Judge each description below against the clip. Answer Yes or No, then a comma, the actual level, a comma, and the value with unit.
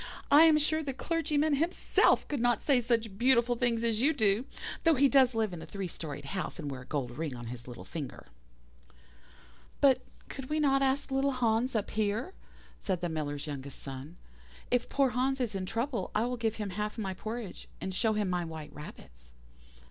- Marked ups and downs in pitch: Yes, wide, 7.6 semitones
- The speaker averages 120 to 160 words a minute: No, average, 200 wpm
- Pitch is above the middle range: Yes, high, 225 Hz